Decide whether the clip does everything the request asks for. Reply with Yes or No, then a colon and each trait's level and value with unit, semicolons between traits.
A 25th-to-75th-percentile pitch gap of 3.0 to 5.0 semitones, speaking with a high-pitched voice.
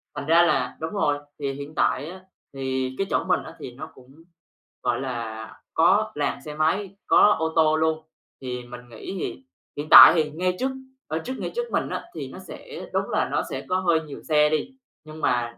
No: average, 4.5 semitones; medium, 155 Hz